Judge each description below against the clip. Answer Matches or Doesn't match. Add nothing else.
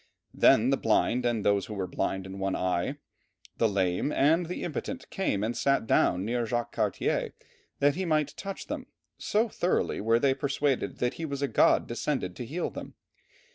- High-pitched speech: Doesn't match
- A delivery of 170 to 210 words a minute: Matches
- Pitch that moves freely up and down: Matches